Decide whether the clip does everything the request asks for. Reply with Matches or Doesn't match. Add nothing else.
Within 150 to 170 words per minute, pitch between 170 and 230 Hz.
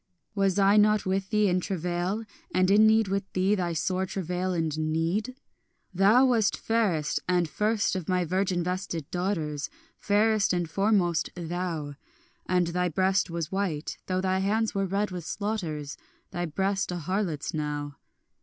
Matches